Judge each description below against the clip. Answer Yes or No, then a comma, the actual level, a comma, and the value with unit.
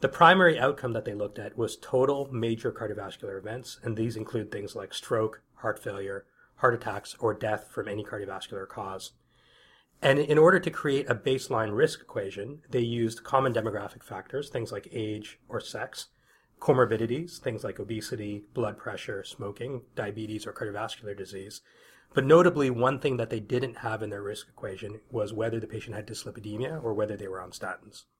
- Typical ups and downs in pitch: Yes, average, 4.0 semitones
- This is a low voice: Yes, low, 115 Hz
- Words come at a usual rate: Yes, average, 175 wpm